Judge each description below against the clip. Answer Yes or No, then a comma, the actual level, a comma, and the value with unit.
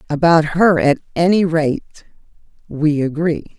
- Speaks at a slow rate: Yes, slow, 115 wpm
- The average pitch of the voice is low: No, medium, 160 Hz